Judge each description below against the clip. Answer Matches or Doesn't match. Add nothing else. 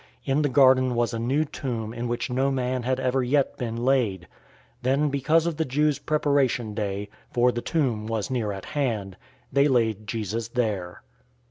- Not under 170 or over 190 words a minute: Matches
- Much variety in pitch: Doesn't match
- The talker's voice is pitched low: Matches